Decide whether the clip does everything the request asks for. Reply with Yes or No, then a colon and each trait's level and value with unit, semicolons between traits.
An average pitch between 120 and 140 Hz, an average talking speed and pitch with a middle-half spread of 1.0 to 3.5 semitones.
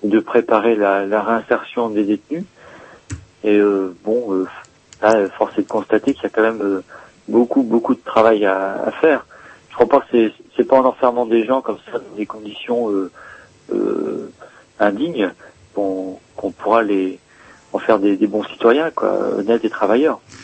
No: low, 110 Hz; average, 180 wpm; average, 3.2 semitones